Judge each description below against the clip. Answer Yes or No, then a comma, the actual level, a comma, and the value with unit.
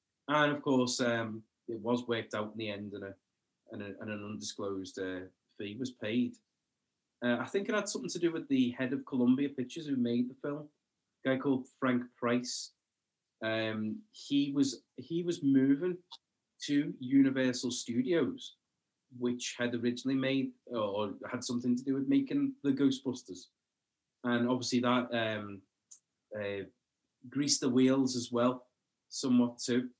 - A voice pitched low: Yes, low, 125 Hz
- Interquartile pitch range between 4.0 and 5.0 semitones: No, narrow, 2.6 semitones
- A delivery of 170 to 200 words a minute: No, average, 160 wpm